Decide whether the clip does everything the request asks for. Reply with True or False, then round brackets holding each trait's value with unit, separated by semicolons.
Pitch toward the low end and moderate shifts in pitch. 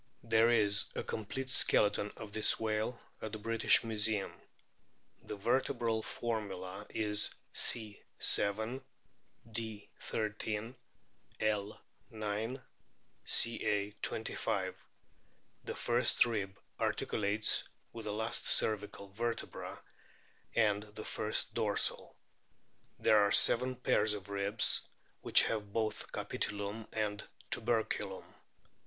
False (110 Hz; 1.7 semitones)